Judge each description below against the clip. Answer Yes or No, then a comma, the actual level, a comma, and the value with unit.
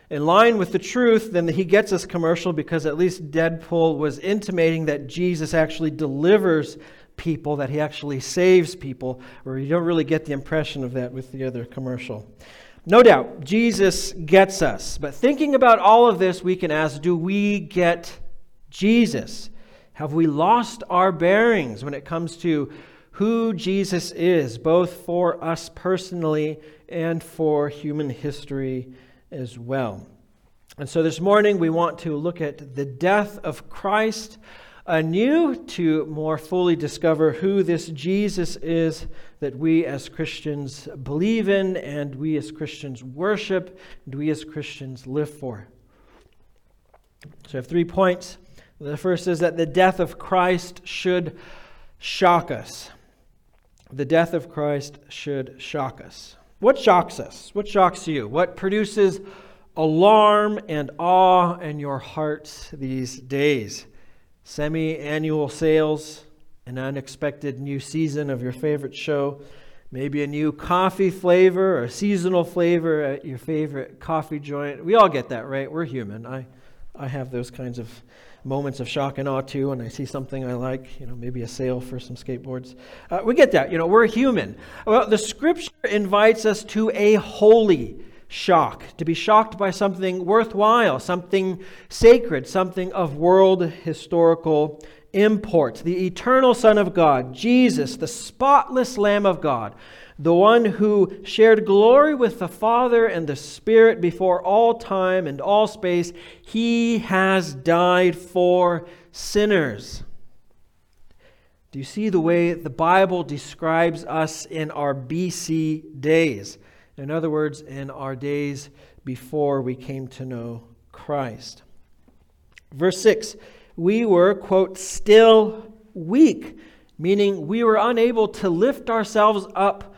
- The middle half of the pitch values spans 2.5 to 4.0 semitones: No, average, 5.0 semitones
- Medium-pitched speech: Yes, medium, 165 Hz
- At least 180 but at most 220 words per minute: No, average, 145 wpm